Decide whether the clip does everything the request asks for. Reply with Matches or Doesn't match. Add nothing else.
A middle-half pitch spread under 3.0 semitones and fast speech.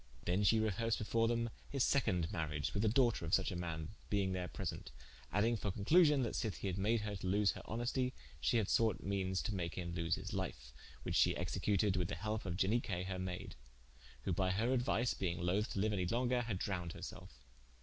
Doesn't match